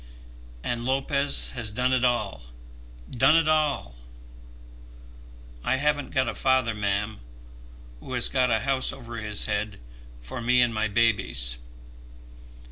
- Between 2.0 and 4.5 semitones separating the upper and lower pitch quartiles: Yes, average, 3.7 semitones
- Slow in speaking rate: Yes, slow, 130 wpm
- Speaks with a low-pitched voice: Yes, low, 120 Hz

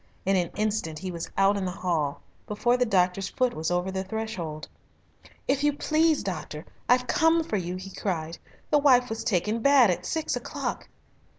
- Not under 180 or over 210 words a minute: Yes, average, 185 wpm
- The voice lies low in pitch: No, high, 195 Hz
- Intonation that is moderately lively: No, wide, 5.8 semitones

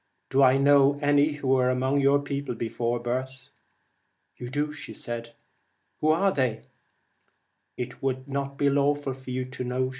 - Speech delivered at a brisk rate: No, average, 160 wpm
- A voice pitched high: No, low, 135 Hz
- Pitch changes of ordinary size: No, narrow, 2.1 semitones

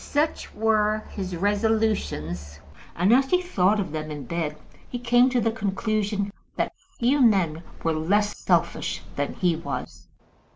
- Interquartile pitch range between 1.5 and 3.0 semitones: No, average, 4.9 semitones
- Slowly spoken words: No, average, 150 wpm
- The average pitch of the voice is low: No, high, 205 Hz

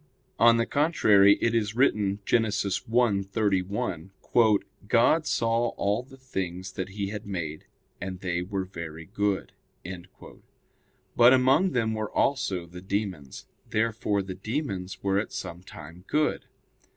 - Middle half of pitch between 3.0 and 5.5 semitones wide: Yes, average, 3.8 semitones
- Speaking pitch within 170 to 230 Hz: No, low, 100 Hz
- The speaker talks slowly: Yes, slow, 130 wpm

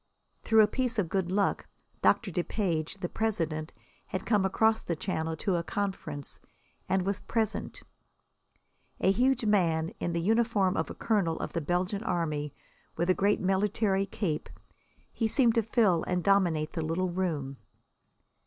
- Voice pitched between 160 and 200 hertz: Yes, high, 190 Hz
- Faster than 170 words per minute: No, average, 155 wpm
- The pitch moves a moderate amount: Yes, average, 4.0 semitones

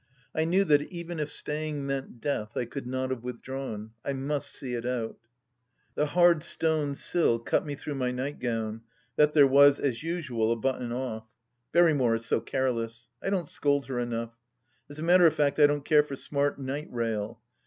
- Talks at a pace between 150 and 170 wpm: No, average, 190 wpm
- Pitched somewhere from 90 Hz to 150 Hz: Yes, low, 135 Hz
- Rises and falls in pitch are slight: No, average, 3.9 semitones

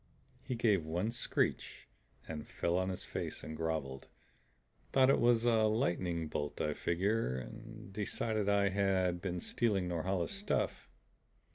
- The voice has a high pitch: No, very low, 95 Hz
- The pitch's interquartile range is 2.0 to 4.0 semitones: No, average, 4.6 semitones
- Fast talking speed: No, slow, 135 wpm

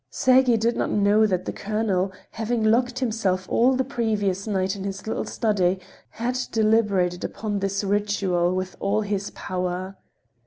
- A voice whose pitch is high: Yes, high, 205 Hz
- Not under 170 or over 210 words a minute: No, average, 155 wpm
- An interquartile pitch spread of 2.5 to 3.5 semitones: Yes, average, 2.9 semitones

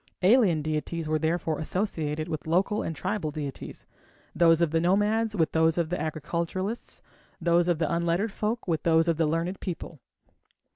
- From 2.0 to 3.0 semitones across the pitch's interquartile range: Yes, average, 2.7 semitones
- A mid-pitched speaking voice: Yes, medium, 170 Hz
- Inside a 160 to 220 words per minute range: Yes, average, 165 wpm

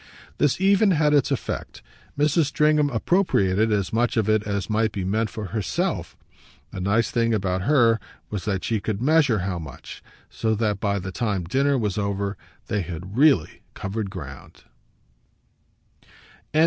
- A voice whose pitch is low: Yes, low, 110 Hz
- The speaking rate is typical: Yes, average, 155 wpm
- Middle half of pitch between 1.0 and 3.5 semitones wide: No, wide, 5.5 semitones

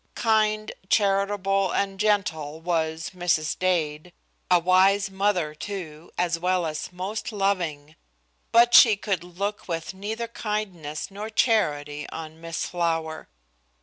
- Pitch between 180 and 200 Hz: Yes, medium, 185 Hz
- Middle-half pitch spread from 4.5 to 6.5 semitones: No, average, 4.0 semitones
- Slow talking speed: Yes, slow, 120 wpm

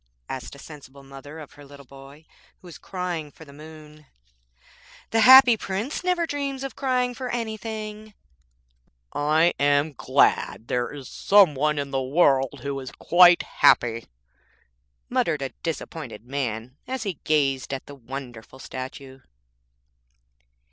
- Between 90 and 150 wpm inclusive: Yes, average, 140 wpm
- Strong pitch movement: Yes, wide, 6.7 semitones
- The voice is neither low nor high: Yes, medium, 150 Hz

